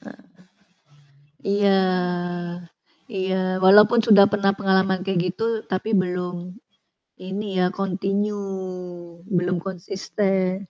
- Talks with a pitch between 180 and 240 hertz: Yes, high, 190 Hz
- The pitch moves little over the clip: Yes, narrow, 1.5 semitones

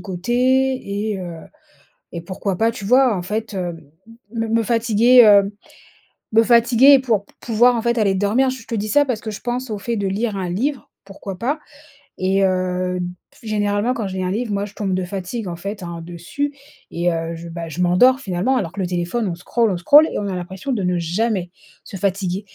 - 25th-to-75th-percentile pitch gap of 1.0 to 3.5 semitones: No, average, 4.3 semitones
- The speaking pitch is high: Yes, high, 205 Hz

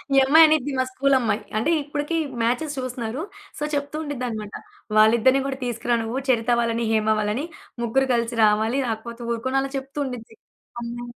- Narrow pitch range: No, average, 3.1 semitones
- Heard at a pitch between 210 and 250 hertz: Yes, high, 245 Hz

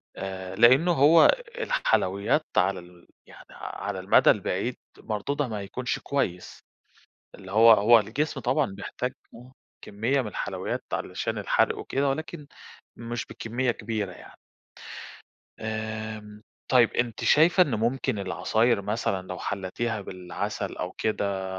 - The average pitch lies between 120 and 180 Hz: No, low, 110 Hz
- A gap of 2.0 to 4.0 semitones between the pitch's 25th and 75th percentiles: No, average, 4.5 semitones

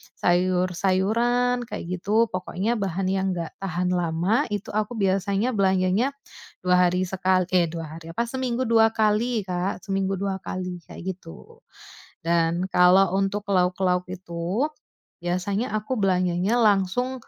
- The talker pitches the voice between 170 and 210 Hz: Yes, high, 190 Hz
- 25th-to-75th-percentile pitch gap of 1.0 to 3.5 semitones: Yes, average, 3.0 semitones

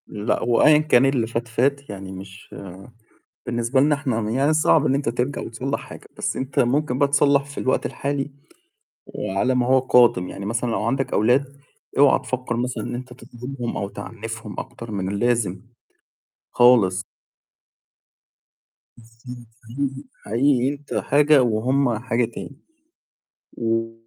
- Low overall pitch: Yes, low, 125 Hz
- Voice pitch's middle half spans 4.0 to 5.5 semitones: No, average, 3.3 semitones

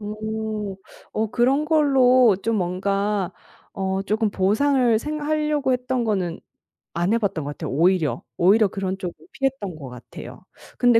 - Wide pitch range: No, average, 5.0 semitones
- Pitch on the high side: Yes, high, 215 Hz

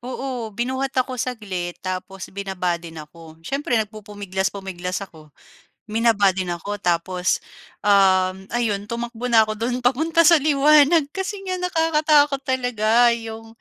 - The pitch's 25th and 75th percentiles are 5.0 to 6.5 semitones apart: Yes, wide, 5.5 semitones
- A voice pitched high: Yes, high, 225 Hz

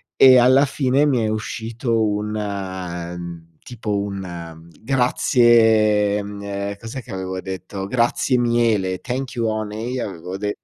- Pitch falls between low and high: No, low, 105 Hz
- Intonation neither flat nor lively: Yes, average, 3.8 semitones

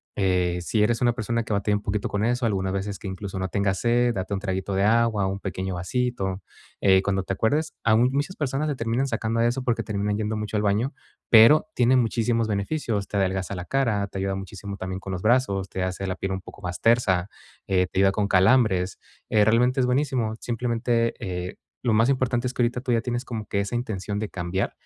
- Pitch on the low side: Yes, low, 105 Hz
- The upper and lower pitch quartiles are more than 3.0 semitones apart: Yes, average, 3.8 semitones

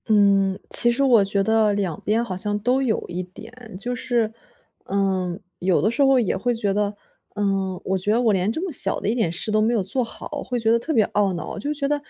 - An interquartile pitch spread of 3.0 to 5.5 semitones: Yes, average, 3.6 semitones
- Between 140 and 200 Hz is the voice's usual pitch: No, high, 210 Hz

